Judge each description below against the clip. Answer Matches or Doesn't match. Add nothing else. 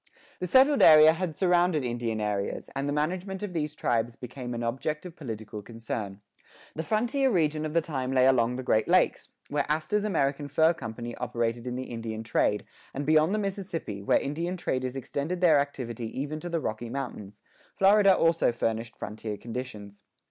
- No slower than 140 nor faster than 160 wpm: Doesn't match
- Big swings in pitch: Matches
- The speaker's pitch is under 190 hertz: Matches